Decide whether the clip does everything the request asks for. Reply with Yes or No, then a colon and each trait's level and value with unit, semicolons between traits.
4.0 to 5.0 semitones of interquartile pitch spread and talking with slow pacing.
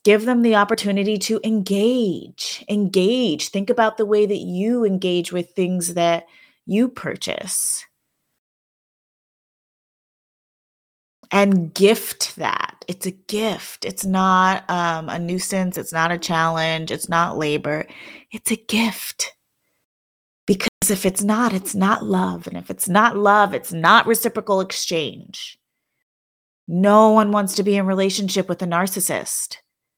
No: average, 3.4 semitones; slow, 130 wpm